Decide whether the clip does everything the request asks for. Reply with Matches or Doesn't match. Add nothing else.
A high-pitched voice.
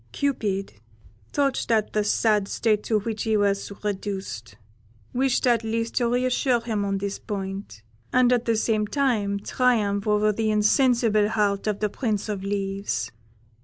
Matches